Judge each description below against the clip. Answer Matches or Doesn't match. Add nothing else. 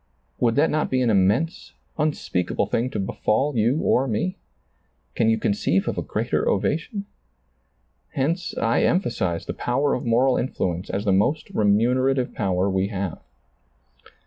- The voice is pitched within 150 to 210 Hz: Doesn't match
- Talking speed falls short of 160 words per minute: Matches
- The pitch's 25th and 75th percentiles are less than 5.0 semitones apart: Doesn't match